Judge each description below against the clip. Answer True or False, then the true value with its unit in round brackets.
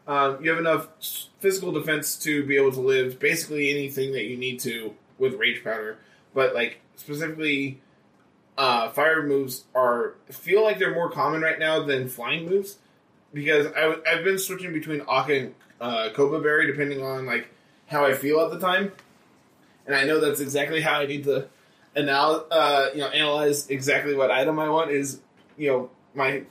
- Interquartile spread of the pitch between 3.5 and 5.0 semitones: False (2.7 semitones)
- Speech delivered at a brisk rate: False (180 wpm)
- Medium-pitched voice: True (145 Hz)